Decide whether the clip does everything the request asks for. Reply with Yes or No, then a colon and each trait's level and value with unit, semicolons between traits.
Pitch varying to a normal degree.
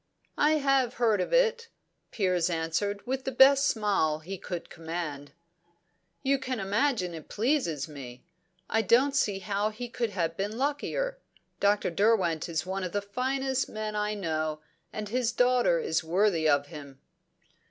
No: wide, 7.3 semitones